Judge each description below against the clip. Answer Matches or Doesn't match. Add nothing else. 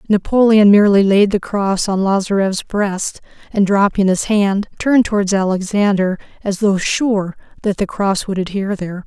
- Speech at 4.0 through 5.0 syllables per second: Matches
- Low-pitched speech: Doesn't match